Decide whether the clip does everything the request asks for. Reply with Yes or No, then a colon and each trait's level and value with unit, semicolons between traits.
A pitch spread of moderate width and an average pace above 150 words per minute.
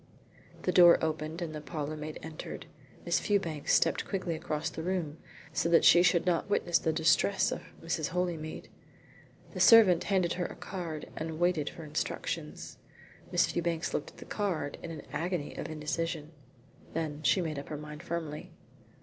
No: narrow, 2.2 semitones; average, 165 wpm